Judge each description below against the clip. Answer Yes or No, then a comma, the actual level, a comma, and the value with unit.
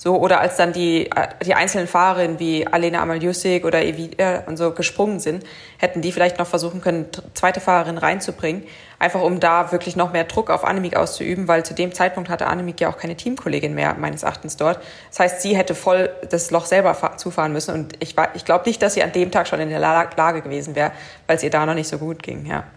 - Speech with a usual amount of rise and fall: No, narrow, 1.9 semitones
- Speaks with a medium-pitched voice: Yes, medium, 170 Hz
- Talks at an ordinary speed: No, fast, 230 wpm